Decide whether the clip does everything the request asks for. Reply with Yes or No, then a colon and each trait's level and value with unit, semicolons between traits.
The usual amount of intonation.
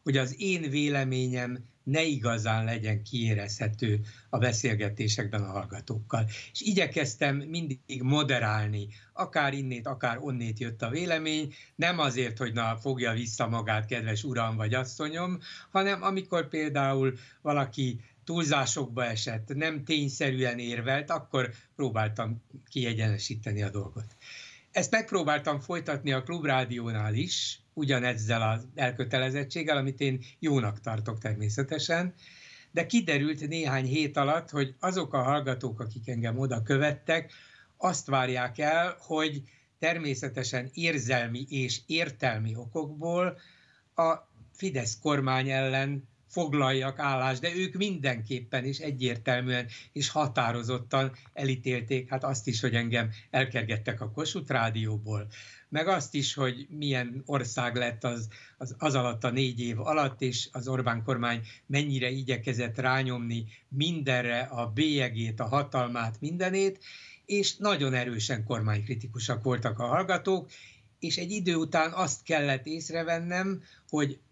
Yes: average, 4.0 semitones